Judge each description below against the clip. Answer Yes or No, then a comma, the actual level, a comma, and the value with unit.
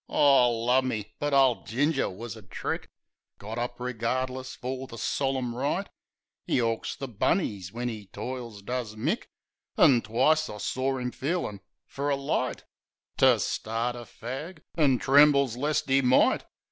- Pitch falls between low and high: No, low, 125 Hz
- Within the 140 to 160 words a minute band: Yes, average, 150 wpm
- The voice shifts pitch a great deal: No, average, 2.9 semitones